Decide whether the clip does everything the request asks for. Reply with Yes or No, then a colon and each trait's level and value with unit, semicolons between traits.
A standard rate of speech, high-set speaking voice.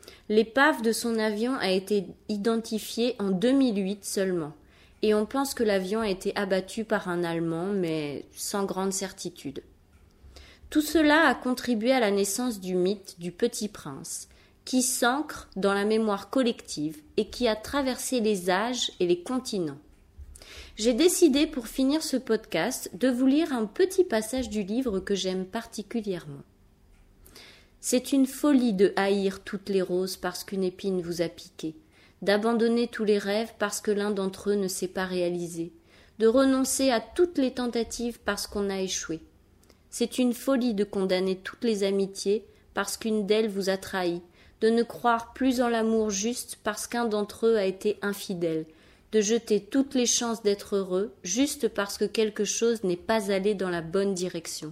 Yes: average, 170 wpm; high, 210 Hz